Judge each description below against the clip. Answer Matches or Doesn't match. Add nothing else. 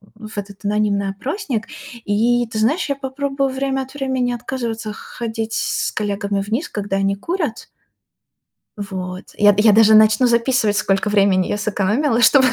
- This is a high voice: Matches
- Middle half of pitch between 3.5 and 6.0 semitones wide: Matches